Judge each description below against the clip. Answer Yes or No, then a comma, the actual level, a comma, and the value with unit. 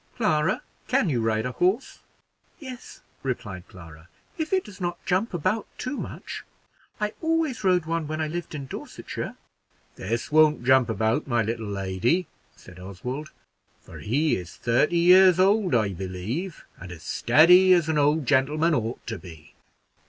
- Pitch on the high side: No, medium, 150 Hz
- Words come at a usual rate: Yes, average, 160 wpm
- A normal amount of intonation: No, wide, 8.3 semitones